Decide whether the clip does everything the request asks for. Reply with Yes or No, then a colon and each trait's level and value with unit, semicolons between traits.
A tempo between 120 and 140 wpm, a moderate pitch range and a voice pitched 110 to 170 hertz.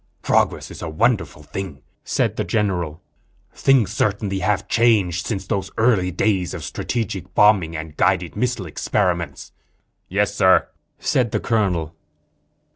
No: slow, 135 wpm; average, 3.5 semitones; very low, 95 Hz